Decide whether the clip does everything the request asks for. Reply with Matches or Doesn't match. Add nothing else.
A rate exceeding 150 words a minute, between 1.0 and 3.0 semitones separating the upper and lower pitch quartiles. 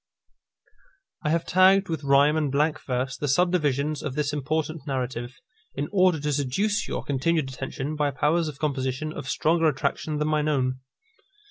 Matches